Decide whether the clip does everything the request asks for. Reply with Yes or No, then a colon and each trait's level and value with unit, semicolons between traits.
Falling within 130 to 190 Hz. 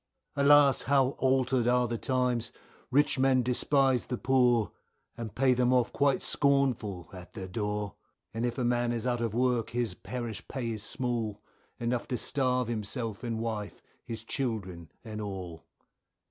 No: low, 120 Hz